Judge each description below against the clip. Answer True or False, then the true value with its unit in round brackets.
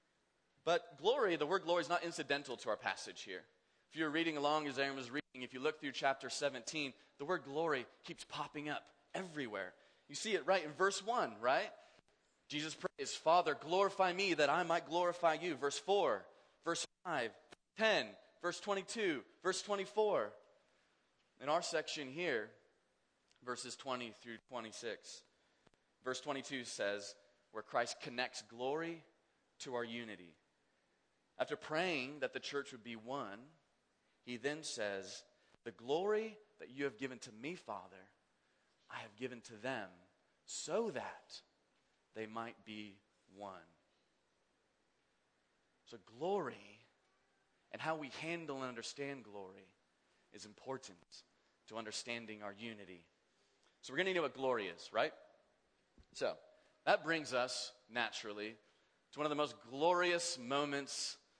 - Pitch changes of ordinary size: False (6.2 semitones)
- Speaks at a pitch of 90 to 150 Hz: True (140 Hz)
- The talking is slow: False (145 wpm)